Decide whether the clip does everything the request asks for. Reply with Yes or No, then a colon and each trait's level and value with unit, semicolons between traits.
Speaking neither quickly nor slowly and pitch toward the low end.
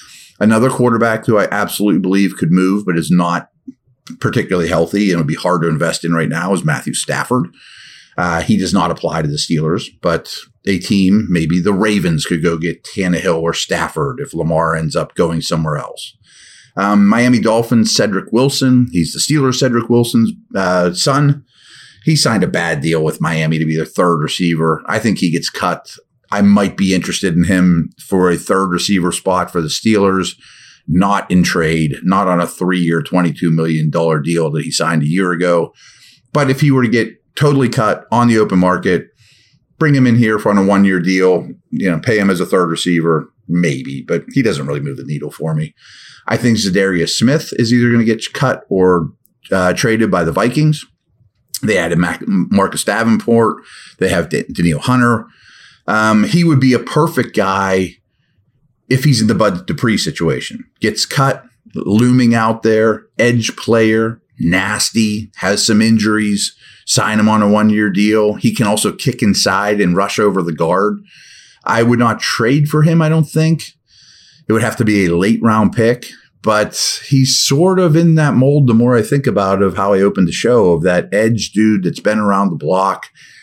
Yes: average, 190 wpm; low, 105 Hz